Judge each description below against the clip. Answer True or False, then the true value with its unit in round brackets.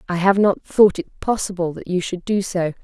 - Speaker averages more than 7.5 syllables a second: False (5.0 syllables/s)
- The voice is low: False (185 Hz)